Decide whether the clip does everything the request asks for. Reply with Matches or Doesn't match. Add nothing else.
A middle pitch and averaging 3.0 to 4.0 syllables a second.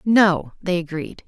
Matches